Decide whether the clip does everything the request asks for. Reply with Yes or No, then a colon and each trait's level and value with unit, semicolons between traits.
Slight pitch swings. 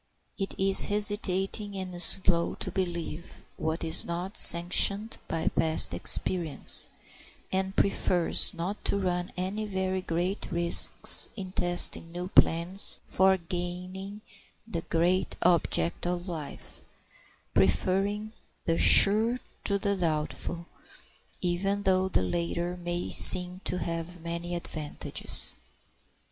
Yes: narrow, 2.2 semitones